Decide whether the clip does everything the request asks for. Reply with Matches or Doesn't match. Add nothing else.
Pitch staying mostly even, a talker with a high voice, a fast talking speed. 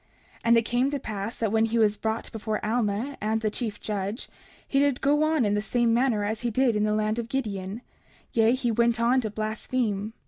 Matches